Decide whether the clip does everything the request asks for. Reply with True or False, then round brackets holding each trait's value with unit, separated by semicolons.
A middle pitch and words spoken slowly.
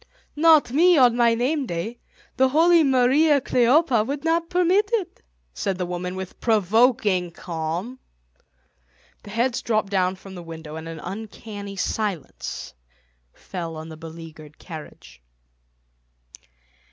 False (215 Hz; 130 wpm)